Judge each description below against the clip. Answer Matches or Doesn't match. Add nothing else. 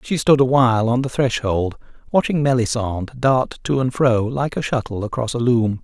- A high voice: Doesn't match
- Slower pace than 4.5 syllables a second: Doesn't match